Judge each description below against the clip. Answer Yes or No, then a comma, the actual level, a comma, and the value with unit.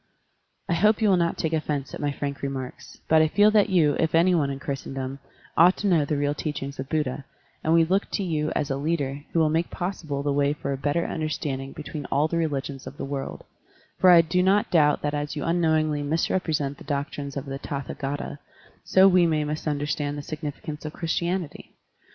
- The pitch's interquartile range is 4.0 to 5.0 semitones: No, average, 2.8 semitones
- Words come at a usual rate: No, fast, 215 wpm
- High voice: No, medium, 150 Hz